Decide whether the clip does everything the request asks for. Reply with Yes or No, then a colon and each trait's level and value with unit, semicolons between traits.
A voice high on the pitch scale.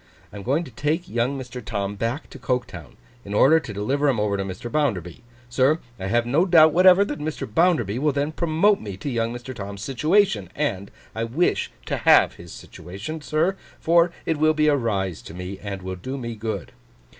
No: low, 125 Hz